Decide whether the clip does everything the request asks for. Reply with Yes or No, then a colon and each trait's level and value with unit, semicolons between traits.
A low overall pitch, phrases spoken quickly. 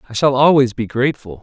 Yes: low, 130 Hz; fast, 210 wpm